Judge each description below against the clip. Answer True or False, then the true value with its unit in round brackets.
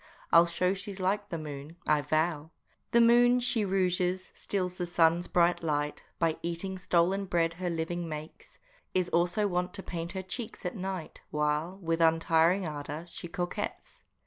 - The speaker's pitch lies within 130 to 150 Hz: False (175 Hz)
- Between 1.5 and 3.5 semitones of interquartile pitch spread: True (2.5 semitones)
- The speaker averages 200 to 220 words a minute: False (165 wpm)